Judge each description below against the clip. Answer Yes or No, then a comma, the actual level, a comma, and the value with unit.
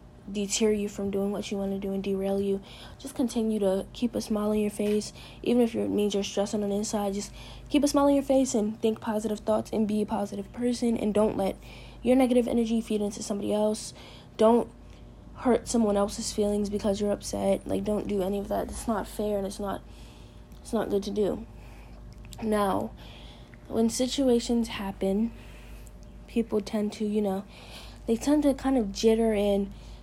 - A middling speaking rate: Yes, average, 195 wpm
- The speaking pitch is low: No, high, 210 Hz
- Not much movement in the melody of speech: Yes, narrow, 2.3 semitones